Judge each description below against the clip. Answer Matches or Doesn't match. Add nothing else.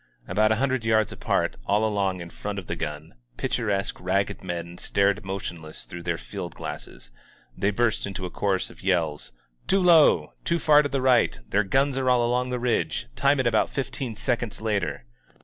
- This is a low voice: Matches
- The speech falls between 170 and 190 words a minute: Matches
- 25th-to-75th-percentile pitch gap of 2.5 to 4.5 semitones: Doesn't match